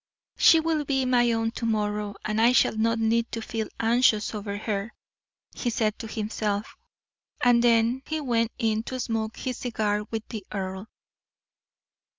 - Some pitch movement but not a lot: No, narrow, 2.1 semitones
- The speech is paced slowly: No, average, 160 wpm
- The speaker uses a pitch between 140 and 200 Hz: No, high, 225 Hz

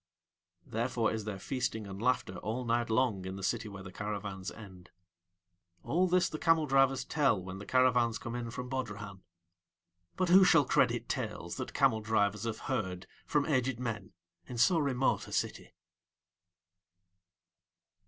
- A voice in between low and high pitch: No, low, 115 Hz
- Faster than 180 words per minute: No, average, 155 wpm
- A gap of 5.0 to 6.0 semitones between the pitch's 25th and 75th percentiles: No, average, 4.4 semitones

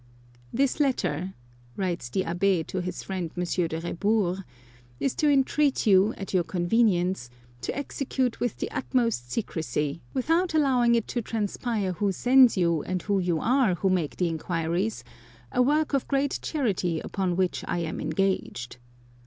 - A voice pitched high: Yes, high, 195 Hz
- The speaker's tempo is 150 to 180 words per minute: Yes, average, 160 wpm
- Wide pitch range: Yes, wide, 6.1 semitones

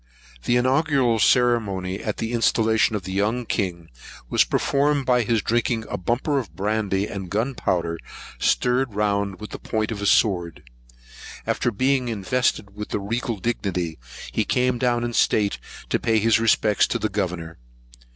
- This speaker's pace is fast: No, average, 160 wpm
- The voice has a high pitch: No, low, 110 Hz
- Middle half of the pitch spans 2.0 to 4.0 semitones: Yes, average, 3.6 semitones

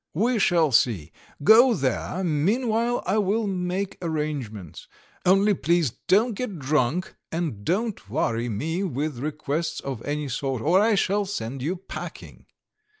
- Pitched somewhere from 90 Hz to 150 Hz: No, medium, 165 Hz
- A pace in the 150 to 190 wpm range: No, average, 140 wpm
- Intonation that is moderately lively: No, wide, 6.4 semitones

